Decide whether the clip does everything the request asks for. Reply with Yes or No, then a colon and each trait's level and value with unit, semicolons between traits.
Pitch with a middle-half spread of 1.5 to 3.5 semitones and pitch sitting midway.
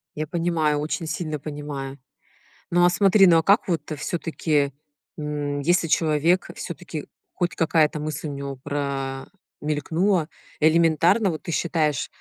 Yes: average, 2.7 semitones; medium, 155 Hz